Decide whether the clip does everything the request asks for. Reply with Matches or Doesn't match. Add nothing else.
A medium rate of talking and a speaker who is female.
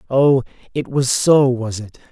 Doesn't match